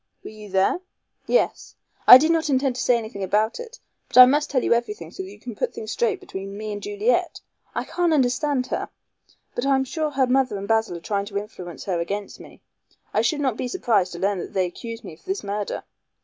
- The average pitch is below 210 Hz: No, high, 235 Hz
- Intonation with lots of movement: Yes, wide, 6.0 semitones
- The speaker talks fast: Yes, fast, 235 wpm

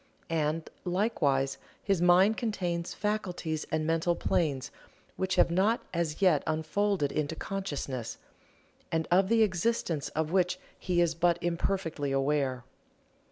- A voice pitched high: No, medium, 170 Hz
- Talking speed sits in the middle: No, slow, 125 wpm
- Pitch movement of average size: Yes, average, 3.8 semitones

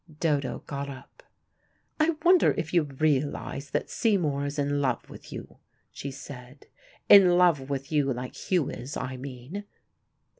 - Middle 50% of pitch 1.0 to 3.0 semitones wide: No, average, 3.4 semitones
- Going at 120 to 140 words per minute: No, average, 150 wpm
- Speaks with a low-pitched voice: No, medium, 145 Hz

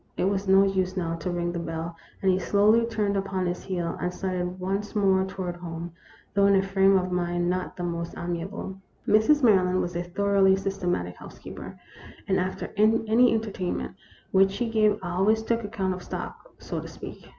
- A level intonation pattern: Yes, narrow, 2.2 semitones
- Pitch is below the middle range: No, high, 190 Hz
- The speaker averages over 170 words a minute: Yes, average, 190 wpm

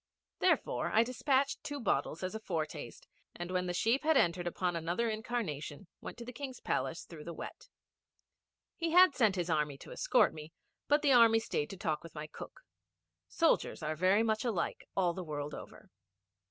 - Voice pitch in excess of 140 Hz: Yes, medium, 185 Hz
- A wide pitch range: Yes, wide, 6.6 semitones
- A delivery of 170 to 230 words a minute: Yes, average, 185 wpm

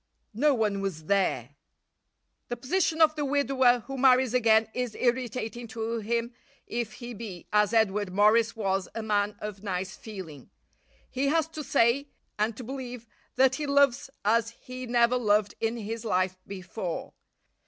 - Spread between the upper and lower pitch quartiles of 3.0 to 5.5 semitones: Yes, average, 3.6 semitones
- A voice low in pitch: No, high, 230 Hz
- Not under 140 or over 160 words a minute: Yes, average, 155 wpm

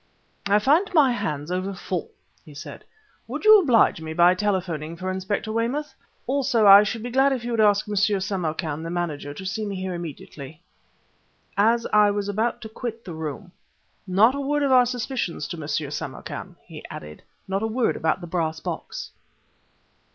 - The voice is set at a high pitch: Yes, high, 200 Hz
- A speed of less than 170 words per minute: No, average, 180 wpm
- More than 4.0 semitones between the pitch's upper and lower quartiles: Yes, wide, 5.5 semitones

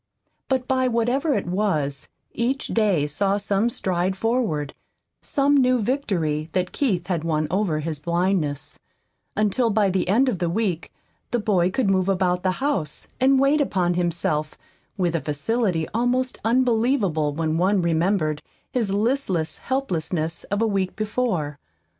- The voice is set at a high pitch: Yes, high, 195 Hz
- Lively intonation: Yes, wide, 6.2 semitones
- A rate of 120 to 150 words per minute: Yes, average, 145 wpm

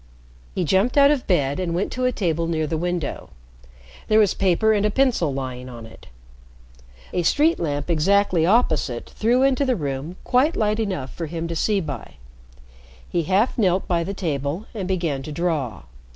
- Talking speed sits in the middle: Yes, average, 180 wpm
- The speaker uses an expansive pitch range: Yes, wide, 5.8 semitones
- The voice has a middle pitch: Yes, medium, 175 Hz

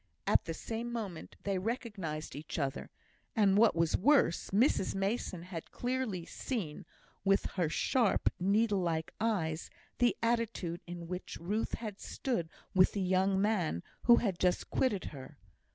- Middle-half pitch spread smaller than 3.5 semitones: No, average, 5.0 semitones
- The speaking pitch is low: No, high, 195 Hz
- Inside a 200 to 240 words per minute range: No, average, 150 wpm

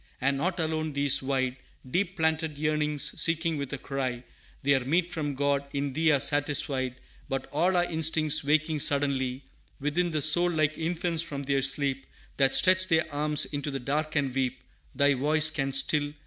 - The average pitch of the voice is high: No, medium, 145 Hz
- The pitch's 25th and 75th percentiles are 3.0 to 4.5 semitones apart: No, narrow, 2.6 semitones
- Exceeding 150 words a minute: Yes, average, 175 wpm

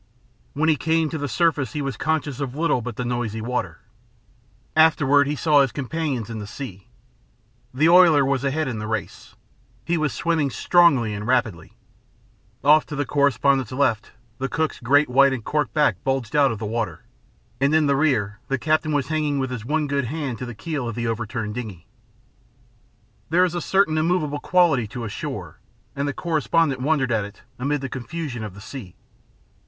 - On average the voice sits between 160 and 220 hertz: No, medium, 140 Hz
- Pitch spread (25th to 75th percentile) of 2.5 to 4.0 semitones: No, average, 4.5 semitones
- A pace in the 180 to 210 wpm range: Yes, average, 190 wpm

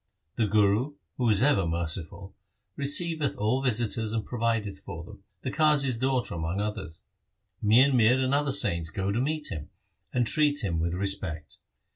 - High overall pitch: No, low, 110 Hz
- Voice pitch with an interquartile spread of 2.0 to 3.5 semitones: No, wide, 5.5 semitones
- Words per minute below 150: No, average, 160 wpm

